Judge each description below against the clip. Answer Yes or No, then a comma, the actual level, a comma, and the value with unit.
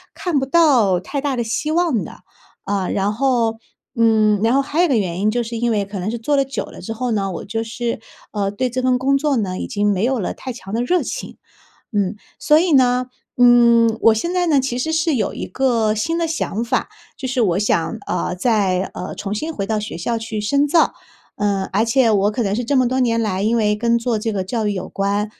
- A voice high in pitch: Yes, high, 230 Hz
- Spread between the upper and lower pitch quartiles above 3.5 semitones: Yes, average, 3.9 semitones